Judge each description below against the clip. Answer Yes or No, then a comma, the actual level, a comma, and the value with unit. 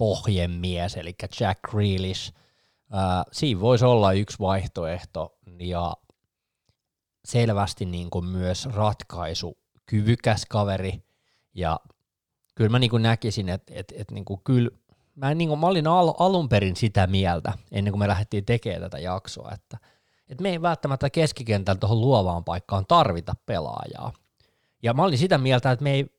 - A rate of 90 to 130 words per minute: No, average, 150 wpm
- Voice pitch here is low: Yes, low, 105 Hz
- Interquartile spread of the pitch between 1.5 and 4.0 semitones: No, average, 4.9 semitones